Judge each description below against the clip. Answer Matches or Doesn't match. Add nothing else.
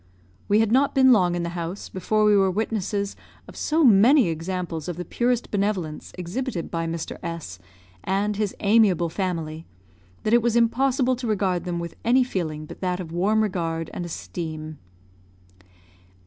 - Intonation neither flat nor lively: Matches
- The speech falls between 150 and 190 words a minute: Matches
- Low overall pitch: Doesn't match